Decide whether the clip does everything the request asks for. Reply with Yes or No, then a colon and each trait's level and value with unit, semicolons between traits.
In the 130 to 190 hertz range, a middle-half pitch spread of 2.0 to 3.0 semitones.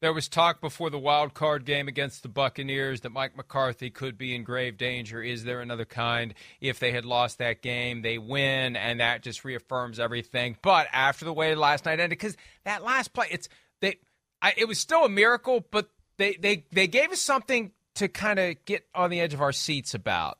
No: medium, 140 Hz; wide, 6.8 semitones